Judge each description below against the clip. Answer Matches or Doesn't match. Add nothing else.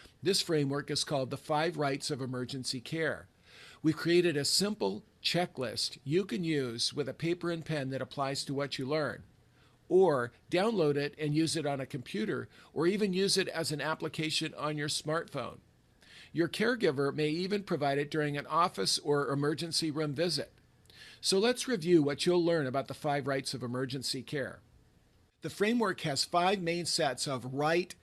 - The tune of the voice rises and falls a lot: Doesn't match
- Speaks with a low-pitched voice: Doesn't match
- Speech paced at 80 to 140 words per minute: Doesn't match